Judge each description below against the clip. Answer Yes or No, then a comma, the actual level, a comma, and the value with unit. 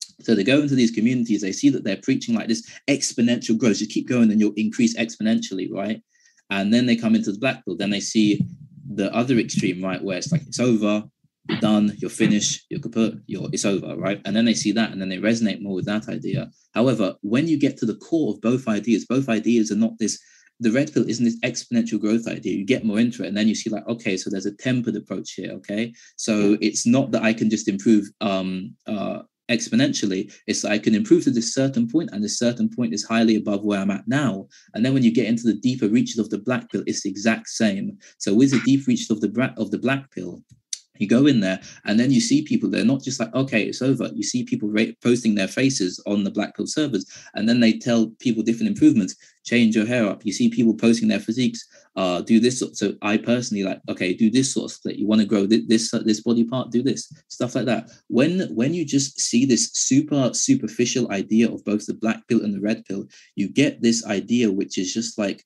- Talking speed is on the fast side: Yes, fast, 240 wpm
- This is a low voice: Yes, low, 115 Hz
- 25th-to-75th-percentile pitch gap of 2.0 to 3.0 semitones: No, average, 3.6 semitones